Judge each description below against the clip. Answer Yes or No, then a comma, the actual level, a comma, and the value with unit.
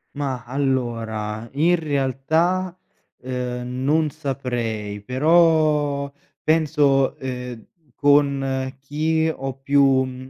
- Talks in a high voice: No, low, 135 Hz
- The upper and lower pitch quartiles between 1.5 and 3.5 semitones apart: Yes, average, 2.9 semitones